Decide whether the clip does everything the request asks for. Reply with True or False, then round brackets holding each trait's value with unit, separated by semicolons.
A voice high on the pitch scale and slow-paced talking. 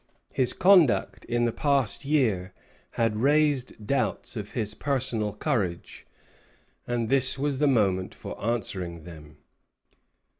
False (120 Hz; 120 wpm)